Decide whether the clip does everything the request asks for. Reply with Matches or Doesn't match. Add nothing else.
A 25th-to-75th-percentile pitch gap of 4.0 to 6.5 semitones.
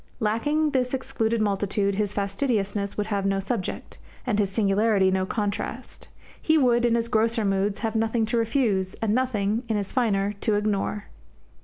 Doesn't match